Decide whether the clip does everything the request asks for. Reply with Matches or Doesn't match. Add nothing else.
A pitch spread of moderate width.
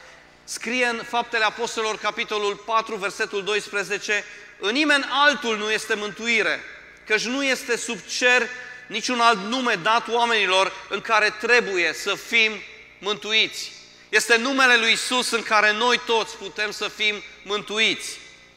Doesn't match